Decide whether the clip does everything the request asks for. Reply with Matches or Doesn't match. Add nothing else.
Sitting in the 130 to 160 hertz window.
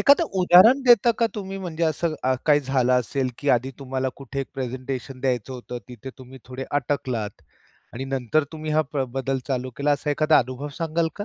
Matches